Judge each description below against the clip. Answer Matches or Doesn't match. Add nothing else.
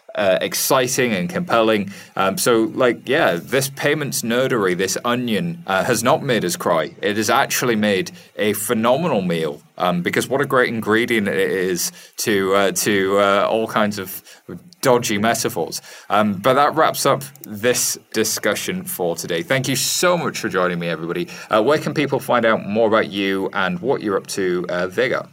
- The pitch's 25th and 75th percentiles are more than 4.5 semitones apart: Matches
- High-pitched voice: Doesn't match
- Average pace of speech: Matches